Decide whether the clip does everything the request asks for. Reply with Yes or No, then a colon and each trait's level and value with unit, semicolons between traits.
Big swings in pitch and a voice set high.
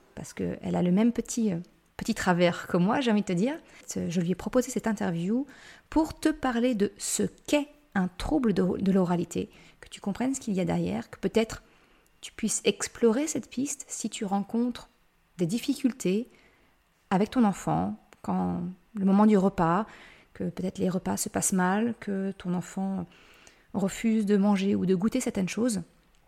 No: average, 4.1 semitones; high, 205 Hz